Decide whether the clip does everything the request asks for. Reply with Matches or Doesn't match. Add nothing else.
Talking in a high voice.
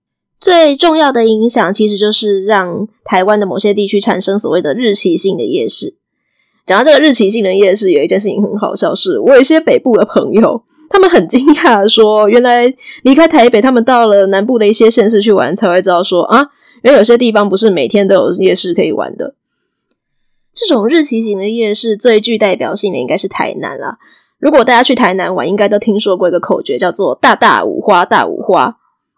Matches